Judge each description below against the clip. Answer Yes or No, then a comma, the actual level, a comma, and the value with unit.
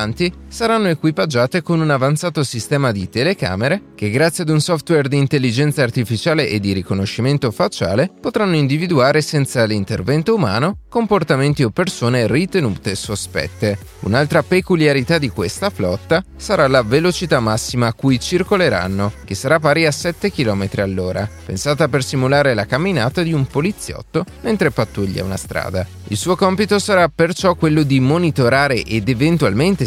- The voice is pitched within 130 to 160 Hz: Yes, medium, 140 Hz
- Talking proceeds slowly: No, average, 145 wpm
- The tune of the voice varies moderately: No, wide, 7.5 semitones